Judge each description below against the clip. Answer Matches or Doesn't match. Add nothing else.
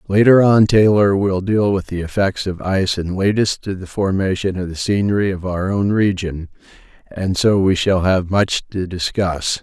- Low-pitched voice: Matches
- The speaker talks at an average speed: Matches